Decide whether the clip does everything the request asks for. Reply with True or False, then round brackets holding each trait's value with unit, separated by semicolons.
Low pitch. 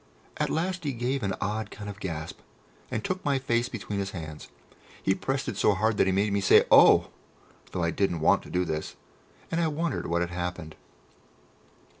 True (100 Hz)